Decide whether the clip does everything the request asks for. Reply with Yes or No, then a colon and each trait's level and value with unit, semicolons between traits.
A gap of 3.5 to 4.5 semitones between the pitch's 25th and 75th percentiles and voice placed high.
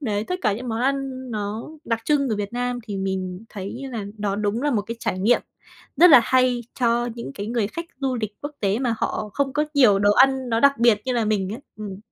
Yes: average, 4.0 semitones; high, 230 Hz